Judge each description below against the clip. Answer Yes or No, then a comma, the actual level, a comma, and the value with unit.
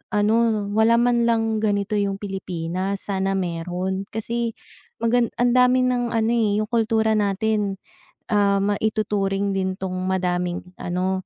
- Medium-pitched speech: No, high, 205 Hz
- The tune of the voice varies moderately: Yes, average, 3.0 semitones